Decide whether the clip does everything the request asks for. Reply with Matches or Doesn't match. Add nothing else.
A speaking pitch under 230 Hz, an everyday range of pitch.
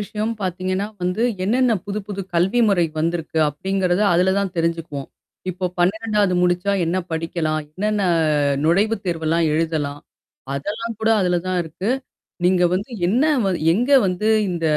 Matches